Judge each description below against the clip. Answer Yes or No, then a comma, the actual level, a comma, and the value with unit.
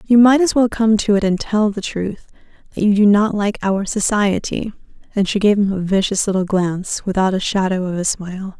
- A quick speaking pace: Yes, fast, 225 wpm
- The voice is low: No, high, 200 Hz